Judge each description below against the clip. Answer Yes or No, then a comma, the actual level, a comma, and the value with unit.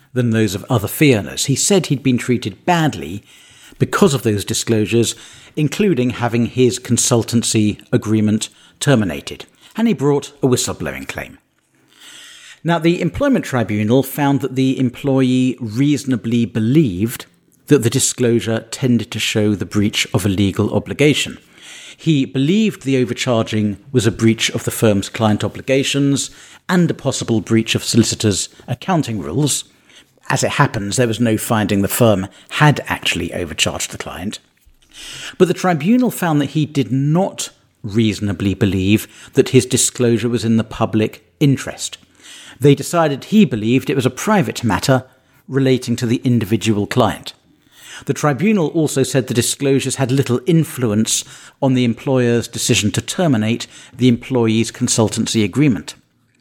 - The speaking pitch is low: Yes, low, 125 Hz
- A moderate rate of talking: Yes, average, 145 wpm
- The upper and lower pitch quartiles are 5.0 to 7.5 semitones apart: No, average, 3.9 semitones